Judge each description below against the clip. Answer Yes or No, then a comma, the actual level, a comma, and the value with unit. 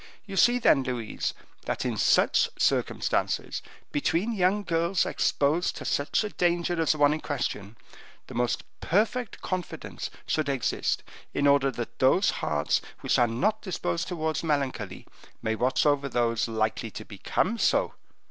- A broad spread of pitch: Yes, wide, 6.8 semitones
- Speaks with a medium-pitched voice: Yes, medium, 145 Hz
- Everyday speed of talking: Yes, average, 150 wpm